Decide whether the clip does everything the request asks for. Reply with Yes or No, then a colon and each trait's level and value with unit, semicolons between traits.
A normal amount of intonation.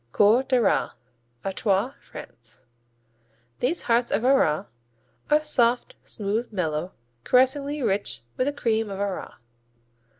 Yes: average, 4.9 semitones